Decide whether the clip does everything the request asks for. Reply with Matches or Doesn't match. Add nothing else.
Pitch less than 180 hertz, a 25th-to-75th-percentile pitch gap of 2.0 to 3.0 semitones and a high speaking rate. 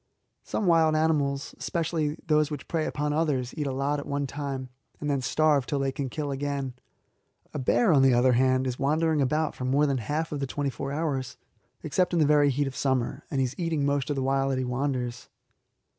Matches